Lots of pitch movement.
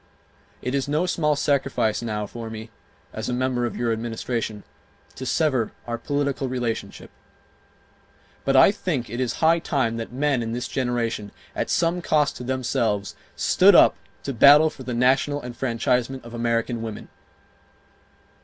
No: average, 3.2 semitones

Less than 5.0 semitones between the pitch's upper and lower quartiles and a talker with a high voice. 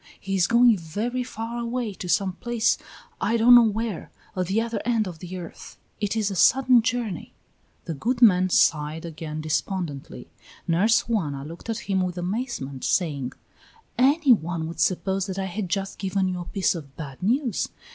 No: average, 5.3 semitones; high, 195 Hz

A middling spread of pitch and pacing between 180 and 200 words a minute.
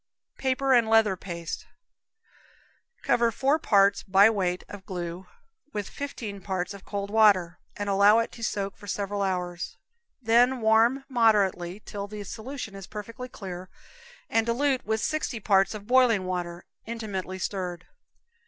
No: average, 3.4 semitones; average, 145 wpm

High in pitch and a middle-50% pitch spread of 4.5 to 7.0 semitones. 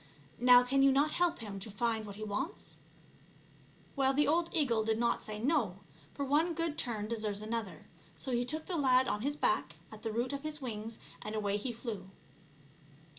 Yes: high, 240 Hz; average, 4.8 semitones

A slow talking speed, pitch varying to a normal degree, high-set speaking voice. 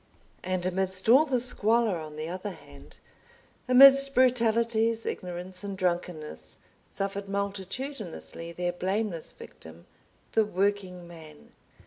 Yes: slow, 110 wpm; average, 4.3 semitones; high, 195 Hz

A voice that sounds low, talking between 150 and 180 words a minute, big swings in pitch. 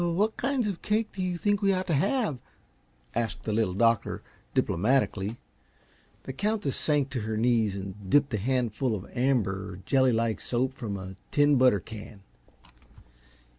Yes: low, 125 Hz; average, 160 wpm; wide, 7.5 semitones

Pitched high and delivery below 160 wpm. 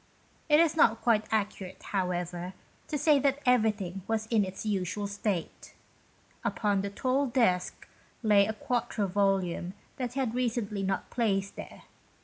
Yes: high, 210 Hz; average, 145 wpm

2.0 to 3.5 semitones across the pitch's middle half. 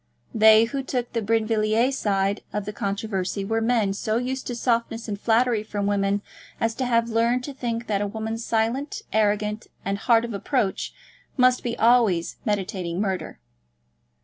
Yes: narrow, 2.5 semitones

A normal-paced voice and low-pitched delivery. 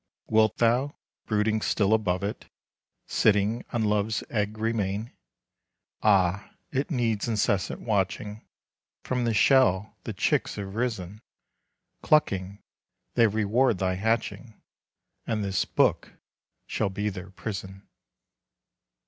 No: slow, 110 wpm; low, 105 Hz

